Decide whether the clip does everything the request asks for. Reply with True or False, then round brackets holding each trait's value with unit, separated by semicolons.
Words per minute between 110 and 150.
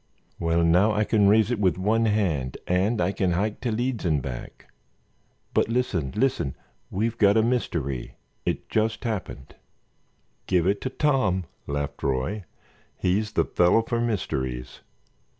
True (140 wpm)